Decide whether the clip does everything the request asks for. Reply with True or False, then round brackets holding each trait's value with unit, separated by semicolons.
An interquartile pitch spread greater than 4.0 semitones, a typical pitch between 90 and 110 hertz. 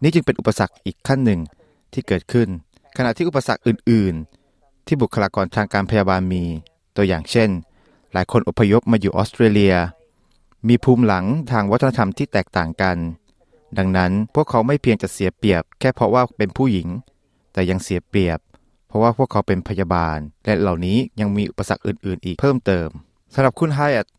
True (4.4 semitones; 100 Hz)